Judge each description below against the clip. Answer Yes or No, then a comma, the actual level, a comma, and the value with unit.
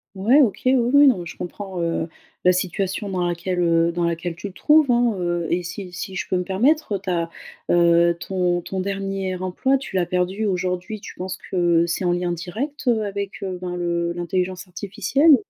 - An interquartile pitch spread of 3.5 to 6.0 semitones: No, average, 2.7 semitones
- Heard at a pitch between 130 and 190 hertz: Yes, medium, 185 Hz